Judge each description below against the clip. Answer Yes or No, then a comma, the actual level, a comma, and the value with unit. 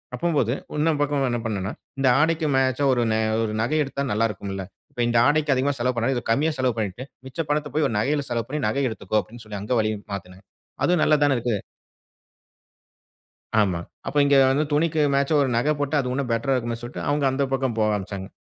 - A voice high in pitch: No, low, 130 Hz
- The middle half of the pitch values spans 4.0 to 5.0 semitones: Yes, average, 4.7 semitones